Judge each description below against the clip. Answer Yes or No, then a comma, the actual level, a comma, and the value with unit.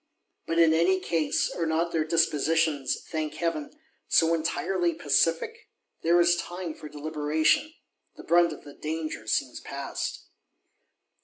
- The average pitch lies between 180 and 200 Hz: No, medium, 165 Hz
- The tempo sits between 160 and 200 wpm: No, slow, 135 wpm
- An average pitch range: No, narrow, 1.7 semitones